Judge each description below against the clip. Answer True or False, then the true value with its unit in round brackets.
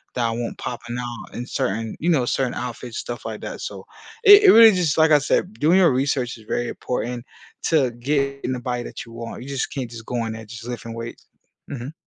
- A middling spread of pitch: True (3.1 semitones)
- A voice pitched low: True (125 Hz)